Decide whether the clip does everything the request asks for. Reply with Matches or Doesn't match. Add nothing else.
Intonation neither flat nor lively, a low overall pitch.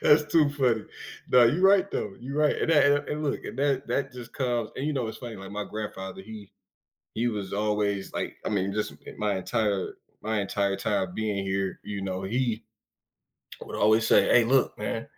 Matches